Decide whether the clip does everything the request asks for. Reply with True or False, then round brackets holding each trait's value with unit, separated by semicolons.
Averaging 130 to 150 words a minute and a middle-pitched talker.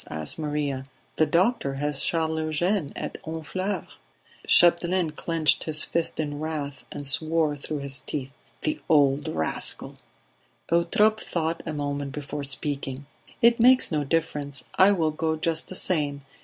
True (140 wpm; 155 Hz)